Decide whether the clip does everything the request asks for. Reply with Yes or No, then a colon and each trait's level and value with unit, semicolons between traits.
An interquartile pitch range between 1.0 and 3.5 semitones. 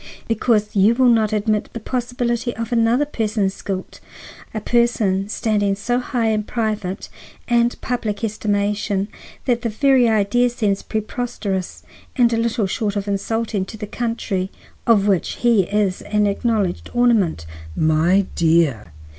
Yes: average, 2.9 semitones